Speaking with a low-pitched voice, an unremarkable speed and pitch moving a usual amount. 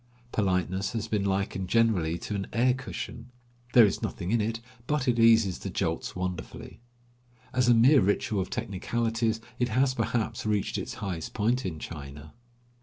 Yes: low, 110 Hz; average, 165 wpm; average, 3.6 semitones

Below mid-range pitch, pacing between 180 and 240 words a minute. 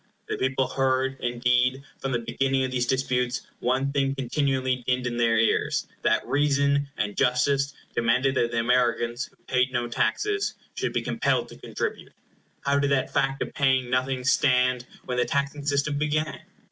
No: low, 130 Hz; average, 170 wpm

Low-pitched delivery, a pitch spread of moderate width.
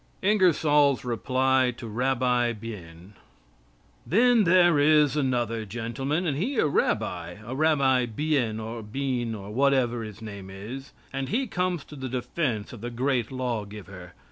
Yes: low, 130 Hz; average, 4.5 semitones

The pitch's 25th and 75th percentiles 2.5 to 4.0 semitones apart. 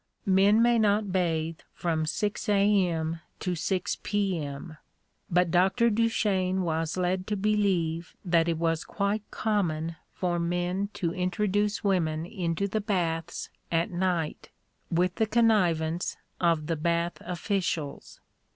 Yes: average, 3.4 semitones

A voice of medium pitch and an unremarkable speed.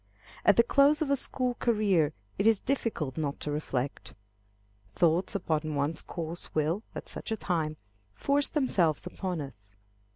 Yes: medium, 170 Hz; average, 155 wpm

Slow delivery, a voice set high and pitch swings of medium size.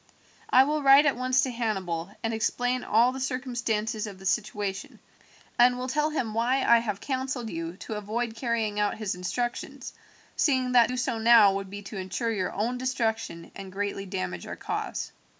No: average, 185 wpm; high, 225 Hz; average, 4.0 semitones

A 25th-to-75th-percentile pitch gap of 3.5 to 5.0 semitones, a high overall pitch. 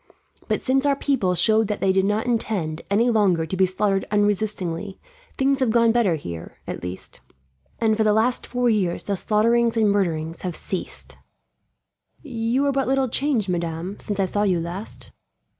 Yes: average, 4.3 semitones; high, 210 Hz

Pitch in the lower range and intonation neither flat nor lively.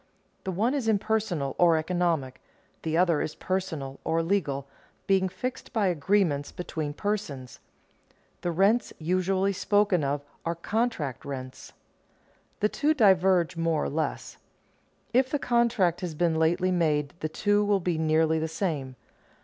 No: medium, 175 Hz; average, 4.4 semitones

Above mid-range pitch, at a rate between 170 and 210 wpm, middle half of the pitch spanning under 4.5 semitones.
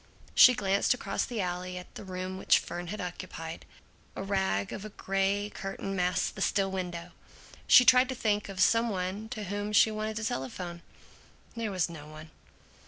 Yes: high, 195 Hz; average, 180 wpm; average, 2.9 semitones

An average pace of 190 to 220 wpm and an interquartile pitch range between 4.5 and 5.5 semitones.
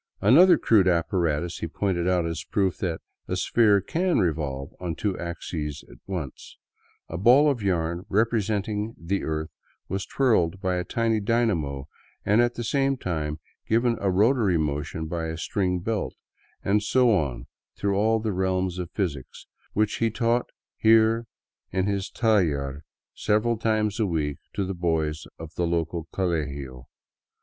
No: average, 165 wpm; average, 5.2 semitones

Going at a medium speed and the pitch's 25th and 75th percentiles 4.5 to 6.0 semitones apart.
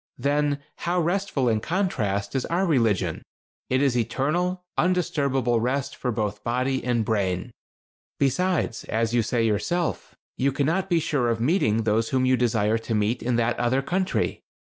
Yes: average, 160 wpm; wide, 5.4 semitones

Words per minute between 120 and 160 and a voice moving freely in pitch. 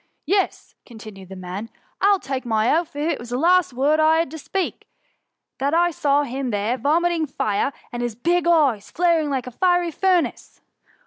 No: average, 200 wpm; wide, 6.1 semitones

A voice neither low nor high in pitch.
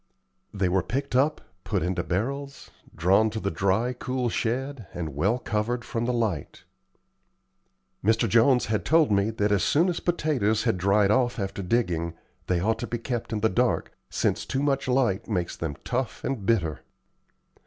No: low, 110 Hz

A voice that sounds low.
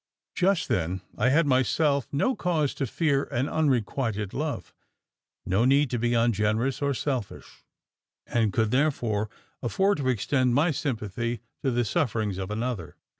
Yes: low, 125 Hz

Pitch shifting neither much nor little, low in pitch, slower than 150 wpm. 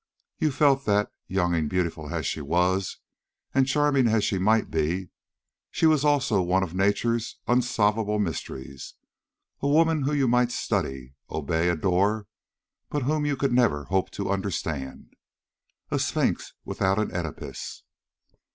No: wide, 6.7 semitones; low, 100 Hz; average, 140 wpm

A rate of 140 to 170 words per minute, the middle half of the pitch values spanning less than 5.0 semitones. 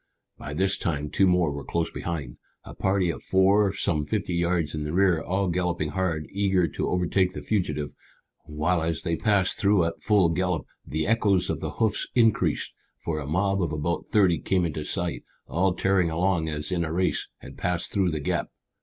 No: average, 195 wpm; average, 3.3 semitones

